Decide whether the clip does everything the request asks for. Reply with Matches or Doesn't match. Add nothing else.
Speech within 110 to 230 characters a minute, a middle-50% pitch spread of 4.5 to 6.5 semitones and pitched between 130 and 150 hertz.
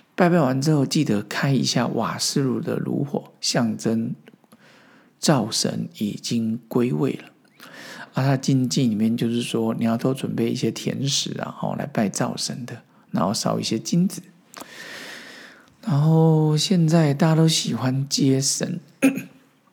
Matches